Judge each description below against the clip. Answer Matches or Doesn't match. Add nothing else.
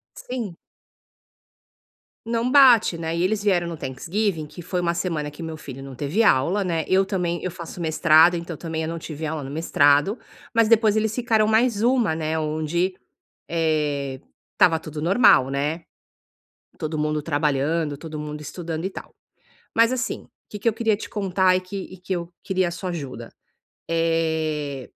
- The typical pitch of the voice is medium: Matches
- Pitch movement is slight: Doesn't match